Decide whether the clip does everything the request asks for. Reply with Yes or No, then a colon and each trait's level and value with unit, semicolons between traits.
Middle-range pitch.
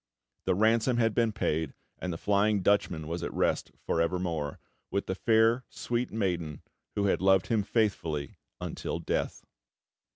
No: low, 100 Hz